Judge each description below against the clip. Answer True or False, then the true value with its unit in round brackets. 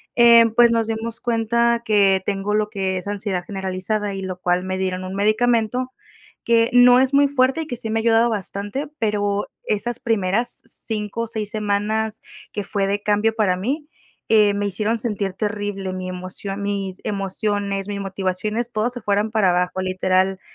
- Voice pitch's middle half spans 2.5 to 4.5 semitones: True (2.8 semitones)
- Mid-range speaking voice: False (210 Hz)